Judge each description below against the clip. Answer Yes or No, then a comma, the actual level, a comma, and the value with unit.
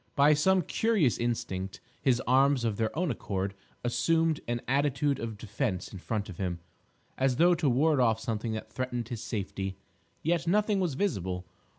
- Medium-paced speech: Yes, average, 170 wpm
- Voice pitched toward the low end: Yes, low, 125 Hz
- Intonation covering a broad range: Yes, wide, 6.0 semitones